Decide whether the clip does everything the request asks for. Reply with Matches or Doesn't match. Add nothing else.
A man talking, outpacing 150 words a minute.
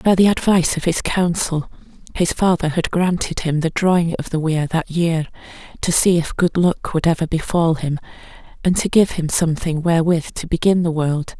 Doesn't match